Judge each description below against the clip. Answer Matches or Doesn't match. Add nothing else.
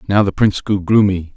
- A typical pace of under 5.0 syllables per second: Doesn't match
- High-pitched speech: Doesn't match